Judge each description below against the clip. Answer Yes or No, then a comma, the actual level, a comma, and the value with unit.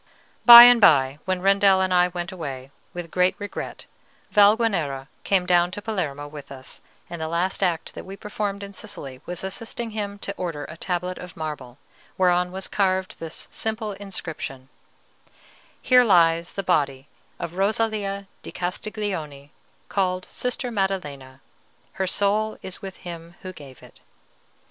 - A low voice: No, medium, 185 Hz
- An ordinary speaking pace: Yes, average, 150 wpm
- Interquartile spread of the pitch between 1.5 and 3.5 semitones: No, average, 4.0 semitones